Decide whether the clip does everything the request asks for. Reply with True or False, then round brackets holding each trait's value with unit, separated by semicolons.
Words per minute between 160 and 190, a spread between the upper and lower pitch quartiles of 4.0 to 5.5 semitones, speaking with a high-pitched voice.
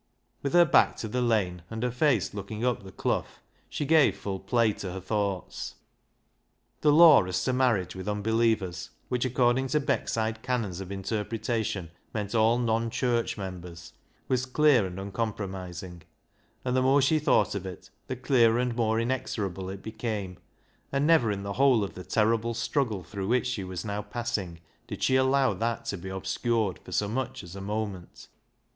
False (180 wpm; 4.3 semitones; 110 Hz)